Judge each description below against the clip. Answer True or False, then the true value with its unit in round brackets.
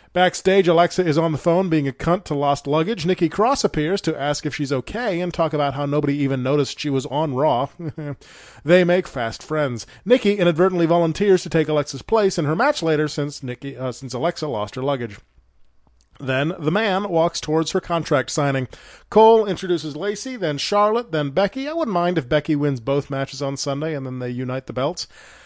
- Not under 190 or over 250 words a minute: True (200 wpm)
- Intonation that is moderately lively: True (4.3 semitones)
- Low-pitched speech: False (155 Hz)